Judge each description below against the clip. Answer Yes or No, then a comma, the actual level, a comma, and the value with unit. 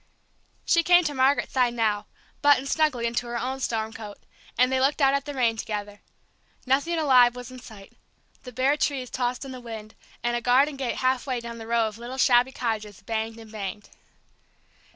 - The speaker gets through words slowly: No, average, 195 wpm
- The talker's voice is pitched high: Yes, high, 245 Hz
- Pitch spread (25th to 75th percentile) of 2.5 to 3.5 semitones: Yes, average, 2.9 semitones